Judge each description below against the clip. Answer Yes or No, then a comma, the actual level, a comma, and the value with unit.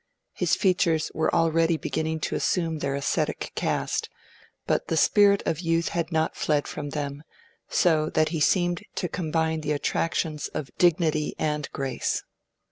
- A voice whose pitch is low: No, medium, 160 Hz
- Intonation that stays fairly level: Yes, narrow, 1.8 semitones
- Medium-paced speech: Yes, average, 155 wpm